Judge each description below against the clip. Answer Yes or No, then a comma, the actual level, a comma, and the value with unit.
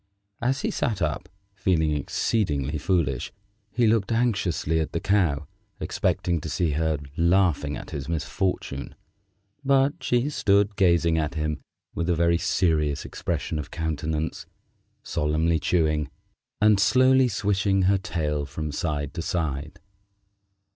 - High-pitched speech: No, very low, 85 Hz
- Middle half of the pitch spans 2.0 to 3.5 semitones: No, average, 4.4 semitones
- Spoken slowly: Yes, slow, 130 wpm